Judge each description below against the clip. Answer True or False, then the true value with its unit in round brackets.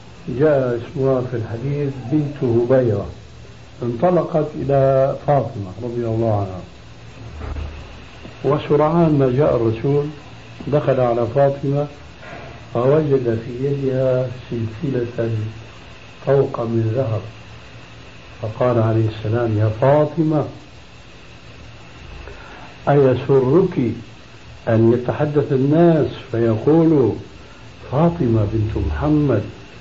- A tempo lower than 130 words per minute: True (80 wpm)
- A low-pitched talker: True (125 Hz)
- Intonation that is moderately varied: True (4.0 semitones)